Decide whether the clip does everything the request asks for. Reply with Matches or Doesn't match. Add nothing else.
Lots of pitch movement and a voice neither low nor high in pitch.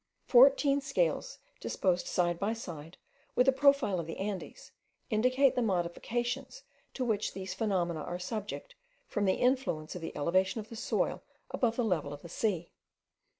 Doesn't match